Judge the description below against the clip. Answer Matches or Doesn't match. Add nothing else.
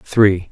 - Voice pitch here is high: Doesn't match